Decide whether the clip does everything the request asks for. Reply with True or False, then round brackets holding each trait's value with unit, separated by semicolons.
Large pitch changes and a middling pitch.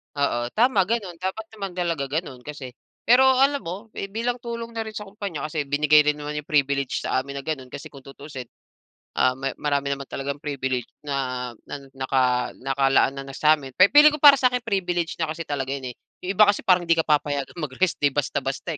True (6.2 semitones; 150 Hz)